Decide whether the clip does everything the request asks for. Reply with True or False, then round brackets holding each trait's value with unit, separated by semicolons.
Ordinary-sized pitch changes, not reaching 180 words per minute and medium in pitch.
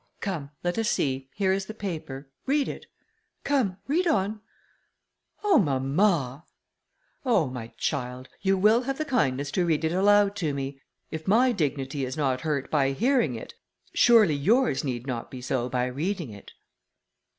False (7.7 semitones; 160 wpm; 160 Hz)